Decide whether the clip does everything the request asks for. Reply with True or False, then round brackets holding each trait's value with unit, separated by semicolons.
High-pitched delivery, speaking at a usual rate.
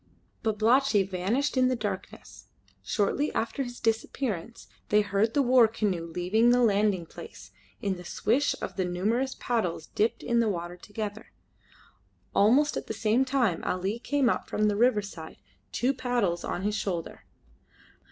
True (215 Hz; 150 wpm)